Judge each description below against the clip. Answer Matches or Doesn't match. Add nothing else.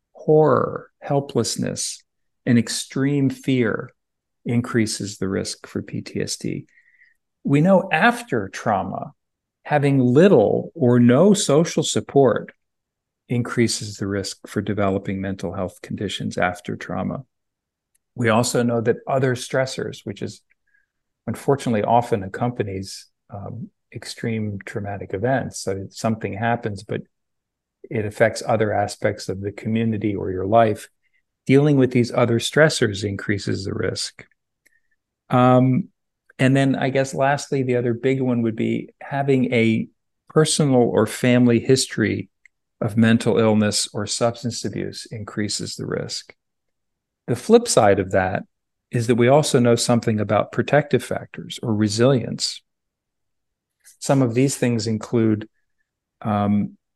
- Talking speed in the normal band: Doesn't match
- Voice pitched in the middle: Doesn't match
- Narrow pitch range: Doesn't match